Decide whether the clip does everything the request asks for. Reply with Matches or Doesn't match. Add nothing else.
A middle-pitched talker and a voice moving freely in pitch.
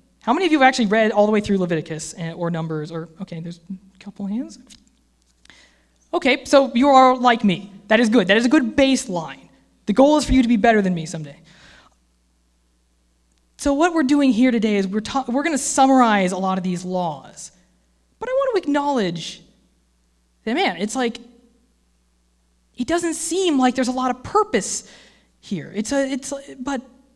Doesn't match